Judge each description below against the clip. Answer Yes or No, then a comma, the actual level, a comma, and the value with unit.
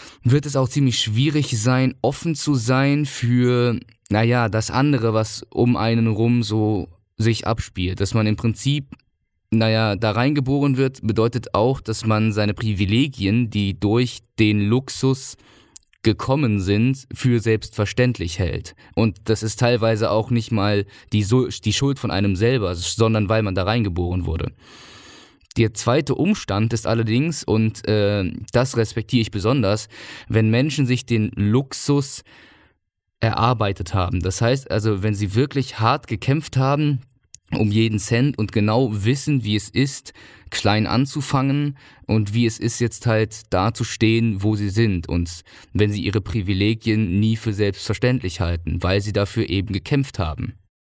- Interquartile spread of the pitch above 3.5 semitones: No, average, 3.2 semitones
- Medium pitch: No, low, 115 Hz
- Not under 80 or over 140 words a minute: No, average, 150 wpm